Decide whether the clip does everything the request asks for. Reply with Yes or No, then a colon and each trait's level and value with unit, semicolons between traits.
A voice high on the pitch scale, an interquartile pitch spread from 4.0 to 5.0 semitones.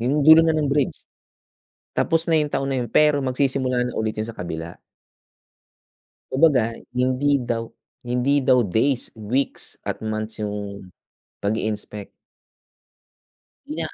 No: low, 125 Hz; average, 4.5 semitones